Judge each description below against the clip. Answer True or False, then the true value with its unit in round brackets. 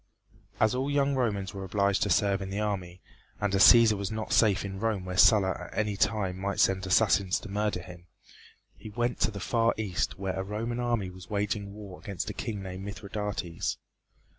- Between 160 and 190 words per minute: False (200 wpm)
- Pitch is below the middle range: True (100 Hz)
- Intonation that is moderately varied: False (2.2 semitones)